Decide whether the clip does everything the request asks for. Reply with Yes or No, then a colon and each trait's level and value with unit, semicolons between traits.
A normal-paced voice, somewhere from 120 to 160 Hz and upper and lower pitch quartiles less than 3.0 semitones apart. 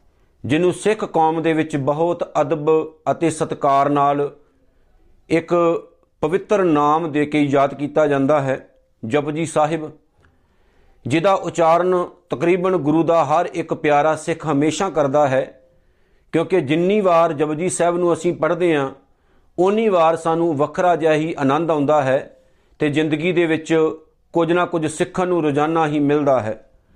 Yes: average, 140 wpm; medium, 155 Hz; narrow, 2.5 semitones